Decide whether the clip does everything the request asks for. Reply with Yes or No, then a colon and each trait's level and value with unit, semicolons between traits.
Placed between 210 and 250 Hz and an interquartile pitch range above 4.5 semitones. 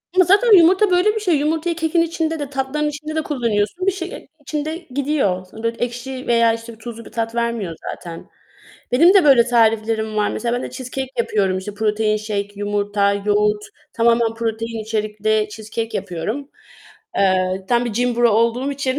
Yes: high, 235 Hz; wide, 5.5 semitones